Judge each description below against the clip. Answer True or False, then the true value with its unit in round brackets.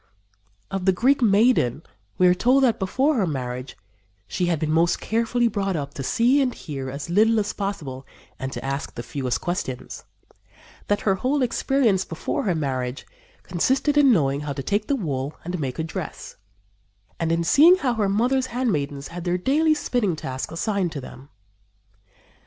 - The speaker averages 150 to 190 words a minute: True (175 wpm)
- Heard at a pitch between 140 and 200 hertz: True (185 Hz)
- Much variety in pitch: True (8.7 semitones)